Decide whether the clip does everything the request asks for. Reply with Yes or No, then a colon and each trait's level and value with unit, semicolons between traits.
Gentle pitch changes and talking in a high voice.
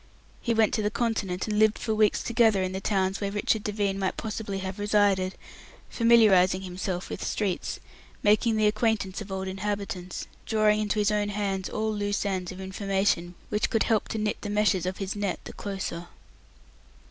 Yes: narrow, 2.0 semitones; high, 205 Hz